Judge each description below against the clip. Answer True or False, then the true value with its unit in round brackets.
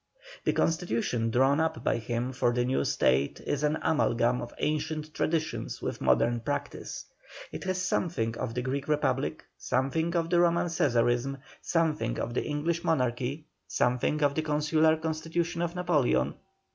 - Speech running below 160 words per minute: True (150 wpm)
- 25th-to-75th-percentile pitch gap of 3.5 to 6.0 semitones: True (4.8 semitones)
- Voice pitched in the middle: True (150 Hz)